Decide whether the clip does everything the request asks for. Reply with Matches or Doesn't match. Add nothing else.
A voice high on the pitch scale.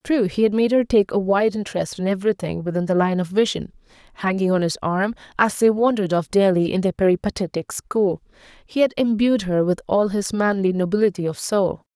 Matches